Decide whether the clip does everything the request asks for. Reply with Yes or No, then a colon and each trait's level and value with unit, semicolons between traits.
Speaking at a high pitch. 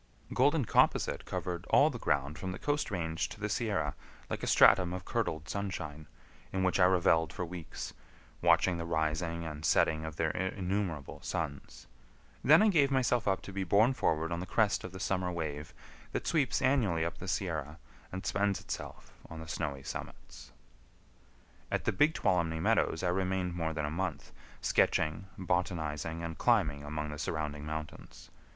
No: very low, 85 Hz